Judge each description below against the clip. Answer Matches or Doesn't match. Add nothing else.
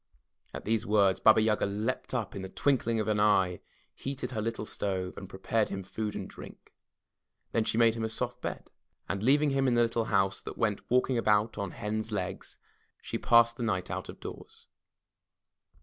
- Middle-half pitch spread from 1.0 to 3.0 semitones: Matches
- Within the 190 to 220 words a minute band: Matches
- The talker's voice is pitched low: Matches